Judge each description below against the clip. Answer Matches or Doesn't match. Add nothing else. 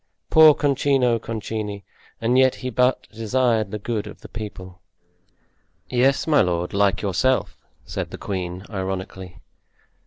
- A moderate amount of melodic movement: Matches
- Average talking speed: Doesn't match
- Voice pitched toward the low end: Matches